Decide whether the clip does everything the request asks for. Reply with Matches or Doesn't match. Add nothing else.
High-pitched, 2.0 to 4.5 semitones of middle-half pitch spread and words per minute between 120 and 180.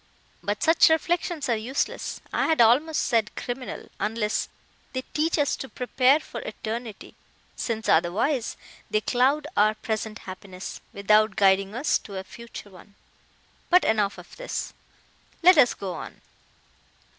Doesn't match